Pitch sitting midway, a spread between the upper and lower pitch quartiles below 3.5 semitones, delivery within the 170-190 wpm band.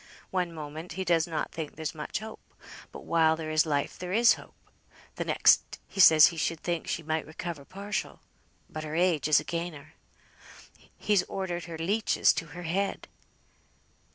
Yes: medium, 165 Hz; narrow, 2.6 semitones; average, 175 wpm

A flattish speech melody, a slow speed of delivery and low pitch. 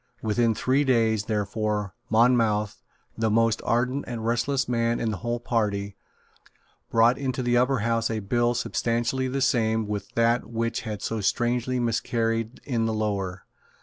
No: narrow, 1.9 semitones; average, 150 wpm; low, 115 Hz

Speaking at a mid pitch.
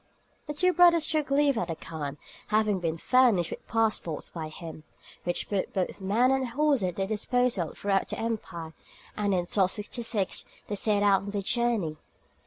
No: high, 205 Hz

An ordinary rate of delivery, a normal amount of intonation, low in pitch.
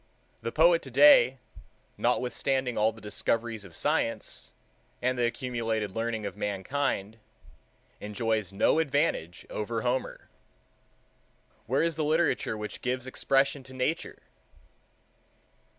No: slow, 110 wpm; average, 3.9 semitones; low, 120 Hz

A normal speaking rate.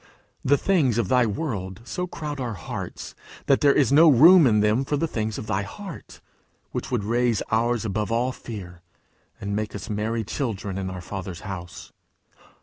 Yes: average, 180 wpm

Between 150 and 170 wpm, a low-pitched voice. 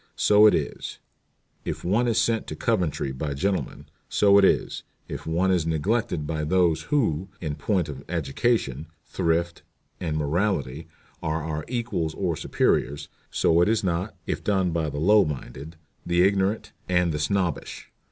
Yes: average, 160 wpm; very low, 85 Hz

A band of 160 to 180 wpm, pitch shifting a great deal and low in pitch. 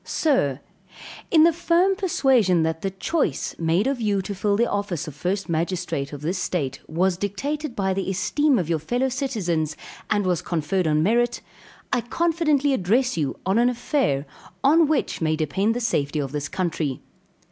No: average, 175 wpm; wide, 8.1 semitones; high, 195 Hz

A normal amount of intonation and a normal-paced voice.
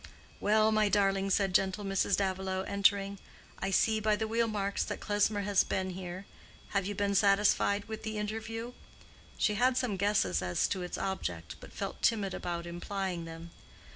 No: narrow, 2.0 semitones; average, 170 wpm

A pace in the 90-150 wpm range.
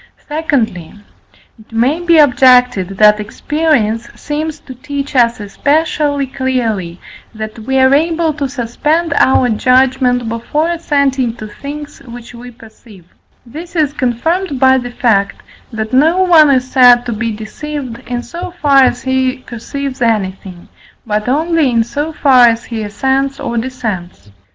Yes: average, 145 wpm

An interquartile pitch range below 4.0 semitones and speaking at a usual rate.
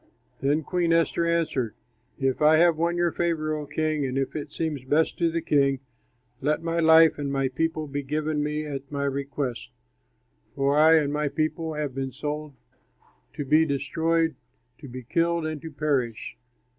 Yes: narrow, 2.6 semitones; average, 175 wpm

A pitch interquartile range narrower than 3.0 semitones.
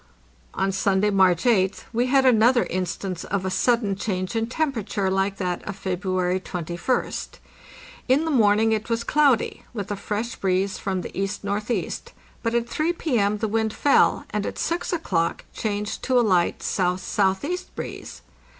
No: average, 3.9 semitones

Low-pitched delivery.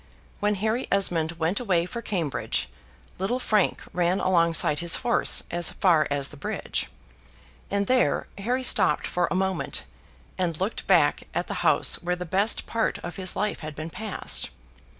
No: medium, 185 Hz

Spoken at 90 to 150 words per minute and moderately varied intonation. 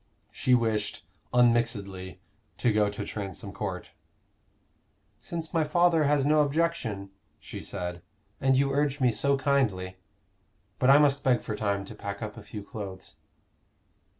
No: average, 145 wpm; wide, 5.7 semitones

